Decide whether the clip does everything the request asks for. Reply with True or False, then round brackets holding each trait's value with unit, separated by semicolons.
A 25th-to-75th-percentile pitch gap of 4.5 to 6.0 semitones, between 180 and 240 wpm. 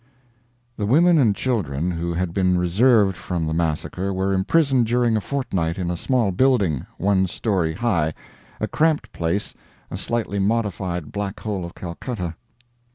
False (5.2 semitones; 155 wpm)